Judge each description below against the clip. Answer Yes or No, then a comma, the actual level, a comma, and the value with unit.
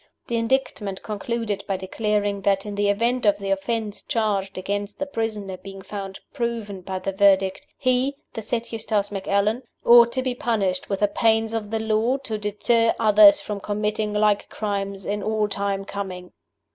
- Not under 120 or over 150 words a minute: No, average, 170 wpm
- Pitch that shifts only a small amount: Yes, narrow, 2.3 semitones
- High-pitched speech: Yes, high, 210 Hz